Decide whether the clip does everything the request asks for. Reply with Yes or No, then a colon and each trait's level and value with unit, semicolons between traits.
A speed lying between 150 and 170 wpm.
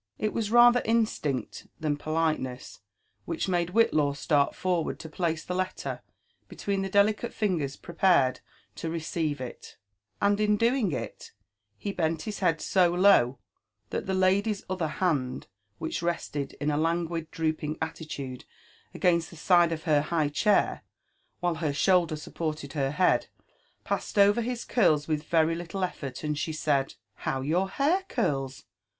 Yes: average, 155 wpm